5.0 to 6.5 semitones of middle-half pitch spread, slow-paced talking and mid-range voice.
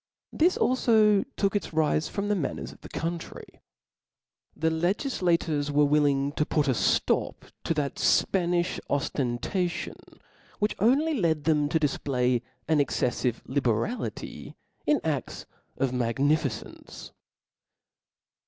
Yes: average, 5.3 semitones; slow, 115 wpm; medium, 155 Hz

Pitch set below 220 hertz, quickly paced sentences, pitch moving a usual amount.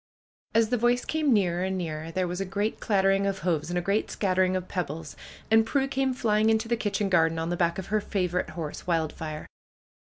Yes: high, 190 Hz; fast, 220 wpm; average, 4.1 semitones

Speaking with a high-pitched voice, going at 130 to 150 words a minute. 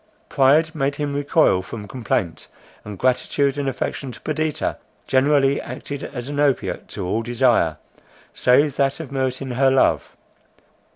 No: low, 135 Hz; average, 140 wpm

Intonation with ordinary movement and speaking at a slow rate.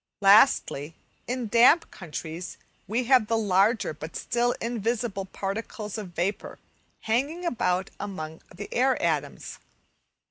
Yes: average, 4.4 semitones; slow, 115 wpm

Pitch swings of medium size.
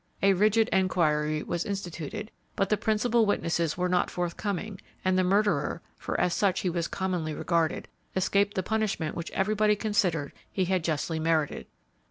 Yes: average, 3.5 semitones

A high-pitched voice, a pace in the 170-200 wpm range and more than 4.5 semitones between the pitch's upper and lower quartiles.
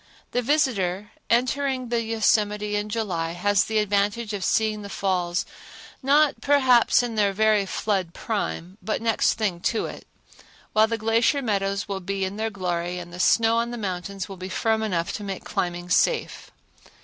No: high, 210 Hz; average, 175 wpm; average, 3.2 semitones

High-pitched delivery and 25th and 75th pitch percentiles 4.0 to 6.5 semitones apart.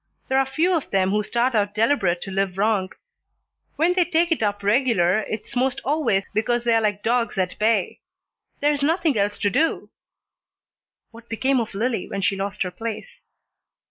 Yes: high, 225 Hz; average, 4.9 semitones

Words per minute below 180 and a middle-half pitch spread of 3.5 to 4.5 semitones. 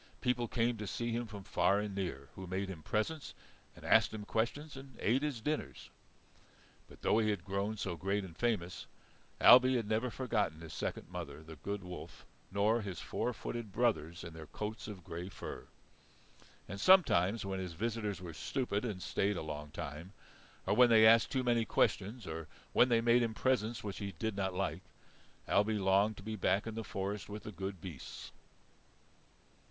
No: average, 190 wpm; average, 3.8 semitones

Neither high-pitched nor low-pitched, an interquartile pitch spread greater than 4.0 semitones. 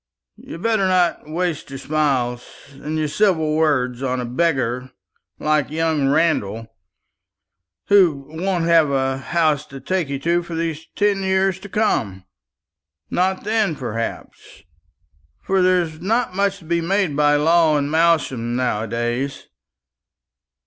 Yes: medium, 155 Hz; average, 5.0 semitones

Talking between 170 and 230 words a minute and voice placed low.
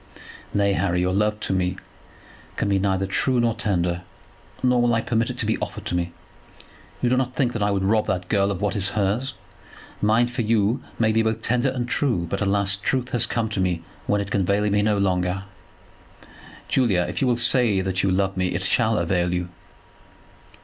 Yes: fast, 205 wpm; low, 105 Hz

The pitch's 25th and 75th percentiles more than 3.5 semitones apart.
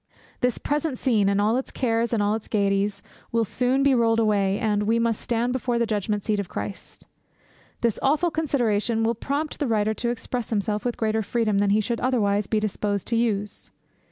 No: average, 2.8 semitones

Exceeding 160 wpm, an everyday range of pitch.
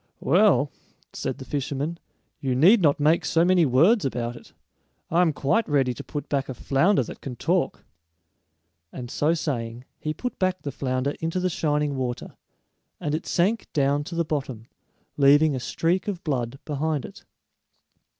Yes: average, 170 wpm; average, 4.0 semitones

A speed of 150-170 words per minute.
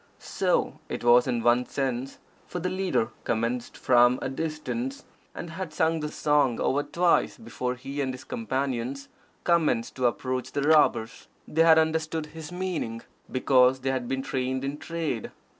Yes: average, 160 wpm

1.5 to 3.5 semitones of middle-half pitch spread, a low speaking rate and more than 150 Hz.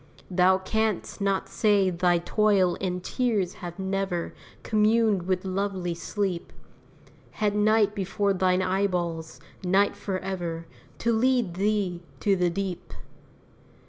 Yes: narrow, 2.5 semitones; slow, 115 wpm; high, 190 Hz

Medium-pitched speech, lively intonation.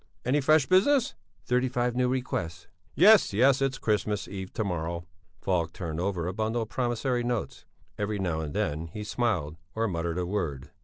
No: low, 105 Hz; wide, 6.5 semitones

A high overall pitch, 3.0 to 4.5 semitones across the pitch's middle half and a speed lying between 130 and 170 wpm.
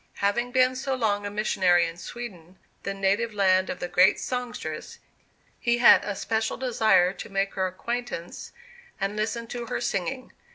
Yes: high, 205 Hz; average, 4.1 semitones; average, 165 wpm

